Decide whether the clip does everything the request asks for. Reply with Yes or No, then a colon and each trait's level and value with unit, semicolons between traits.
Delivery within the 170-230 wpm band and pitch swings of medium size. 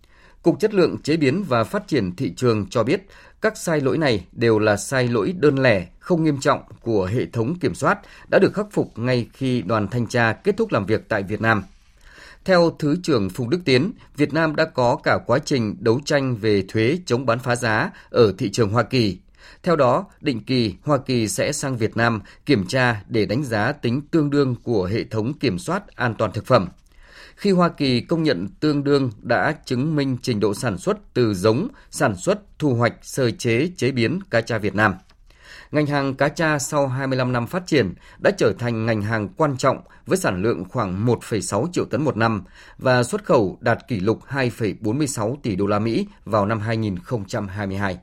Yes: average, 205 wpm; average, 4.8 semitones